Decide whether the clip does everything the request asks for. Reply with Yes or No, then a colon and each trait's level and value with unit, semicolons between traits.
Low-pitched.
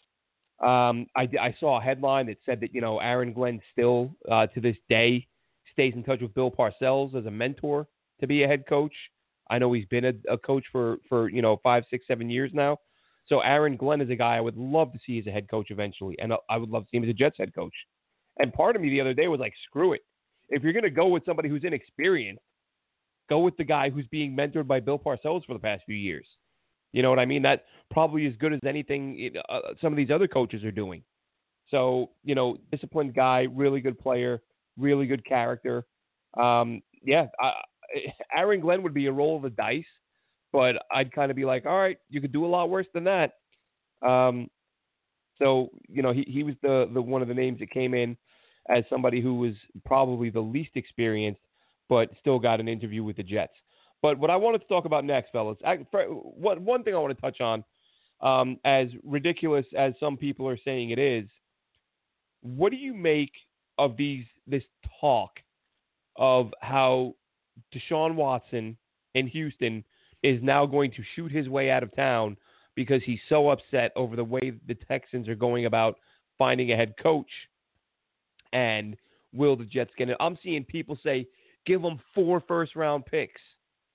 Yes: low, 130 Hz